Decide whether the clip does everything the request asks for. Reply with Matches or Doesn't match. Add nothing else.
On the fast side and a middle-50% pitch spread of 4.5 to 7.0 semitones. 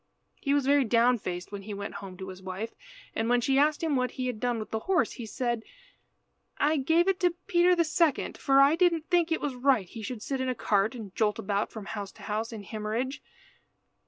Matches